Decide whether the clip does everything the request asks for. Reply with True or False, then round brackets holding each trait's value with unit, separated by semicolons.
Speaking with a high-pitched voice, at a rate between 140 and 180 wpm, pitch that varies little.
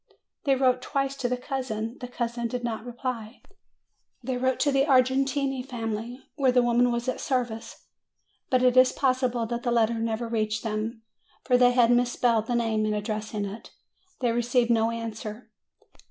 True (240 Hz; 170 wpm; 2.1 semitones)